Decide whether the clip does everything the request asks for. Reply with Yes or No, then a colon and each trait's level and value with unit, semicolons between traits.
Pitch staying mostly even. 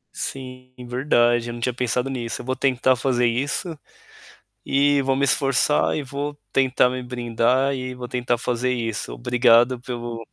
Yes: narrow, 1.9 semitones